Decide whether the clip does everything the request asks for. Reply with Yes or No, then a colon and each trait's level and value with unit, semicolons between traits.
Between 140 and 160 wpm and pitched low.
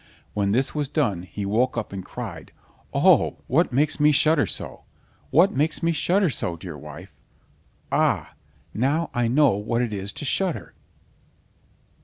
Yes: average, 150 wpm; low, 125 Hz